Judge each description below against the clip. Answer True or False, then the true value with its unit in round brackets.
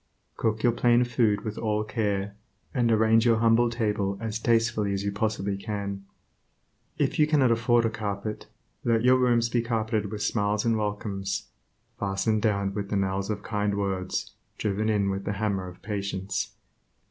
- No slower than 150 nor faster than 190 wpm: True (170 wpm)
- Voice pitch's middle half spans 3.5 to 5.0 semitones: False (2.4 semitones)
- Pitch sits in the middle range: False (105 Hz)